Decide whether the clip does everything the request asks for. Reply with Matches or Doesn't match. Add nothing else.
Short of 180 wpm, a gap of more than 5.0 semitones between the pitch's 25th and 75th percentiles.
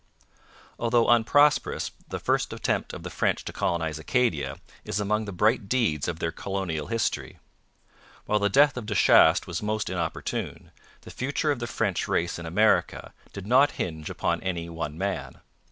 Matches